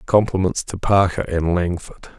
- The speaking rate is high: No, slow, 135 wpm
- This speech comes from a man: Yes, male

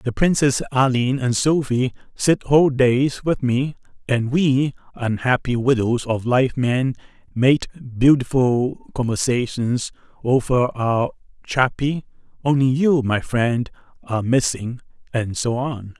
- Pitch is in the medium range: No, low, 125 Hz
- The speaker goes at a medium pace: No, slow, 120 wpm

